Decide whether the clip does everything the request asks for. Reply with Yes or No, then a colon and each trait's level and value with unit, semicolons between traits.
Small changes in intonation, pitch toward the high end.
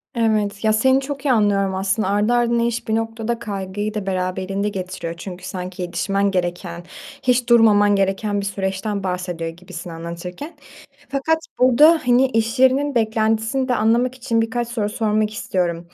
No: average, 3.9 semitones; high, 210 Hz